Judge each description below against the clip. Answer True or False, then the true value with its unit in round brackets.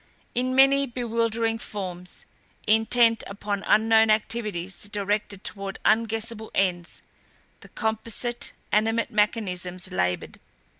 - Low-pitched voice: False (215 Hz)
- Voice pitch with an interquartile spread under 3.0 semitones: True (2.6 semitones)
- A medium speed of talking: False (95 wpm)